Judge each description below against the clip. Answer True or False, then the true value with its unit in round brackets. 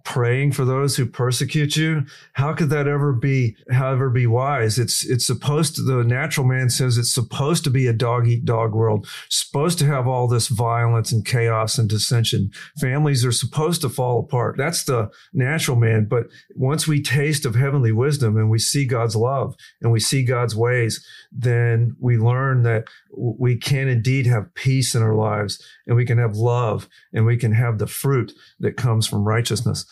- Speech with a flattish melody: False (3.0 semitones)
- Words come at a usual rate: True (185 wpm)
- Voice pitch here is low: True (125 Hz)